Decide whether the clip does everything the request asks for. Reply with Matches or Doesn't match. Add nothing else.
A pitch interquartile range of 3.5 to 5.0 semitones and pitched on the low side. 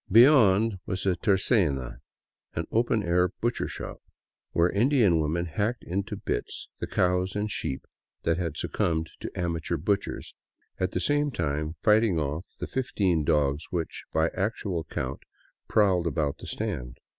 Matches